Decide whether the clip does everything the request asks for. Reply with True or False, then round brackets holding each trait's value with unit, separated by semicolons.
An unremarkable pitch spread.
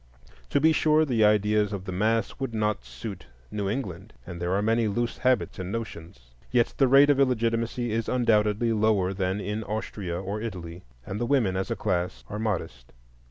True (3.4 semitones)